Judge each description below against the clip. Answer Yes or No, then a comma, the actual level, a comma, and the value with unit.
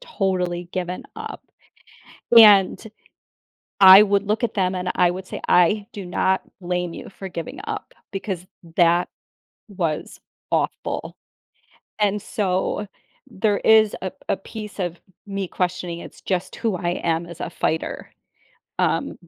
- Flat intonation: Yes, narrow, 2.3 semitones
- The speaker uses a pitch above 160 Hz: Yes, medium, 185 Hz